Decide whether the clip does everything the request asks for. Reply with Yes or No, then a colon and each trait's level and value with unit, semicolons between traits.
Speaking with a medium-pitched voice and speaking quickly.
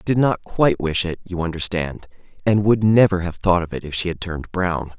No: very low, 90 Hz; fast, 240 wpm